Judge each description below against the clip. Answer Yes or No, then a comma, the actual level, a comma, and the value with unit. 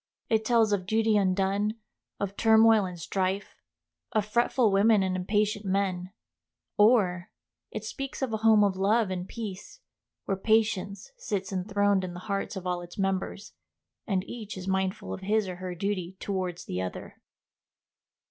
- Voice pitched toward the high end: Yes, high, 200 Hz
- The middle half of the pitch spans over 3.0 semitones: No, narrow, 2.6 semitones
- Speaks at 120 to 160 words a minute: Yes, average, 155 wpm